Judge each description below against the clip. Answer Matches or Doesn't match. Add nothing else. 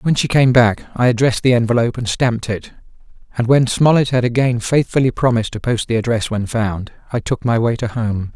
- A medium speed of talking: Doesn't match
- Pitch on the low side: Matches